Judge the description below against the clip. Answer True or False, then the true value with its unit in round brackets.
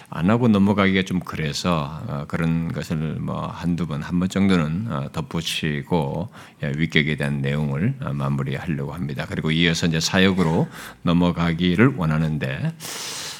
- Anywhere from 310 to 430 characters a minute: False (300 characters per minute)